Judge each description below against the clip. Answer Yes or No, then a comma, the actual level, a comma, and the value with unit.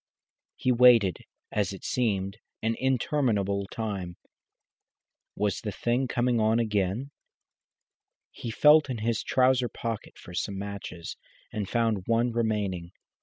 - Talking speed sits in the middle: No, slow, 120 wpm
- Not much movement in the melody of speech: No, average, 3.5 semitones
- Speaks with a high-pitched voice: No, low, 110 Hz